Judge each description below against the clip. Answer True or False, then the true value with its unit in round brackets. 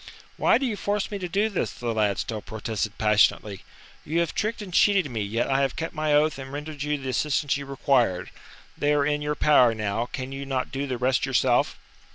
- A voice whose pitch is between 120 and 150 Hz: True (140 Hz)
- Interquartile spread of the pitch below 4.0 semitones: False (4.7 semitones)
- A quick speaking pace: True (220 wpm)